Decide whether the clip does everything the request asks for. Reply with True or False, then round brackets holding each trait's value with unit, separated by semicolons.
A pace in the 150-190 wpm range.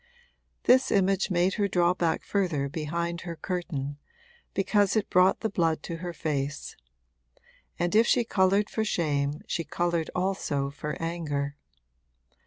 False (140 wpm)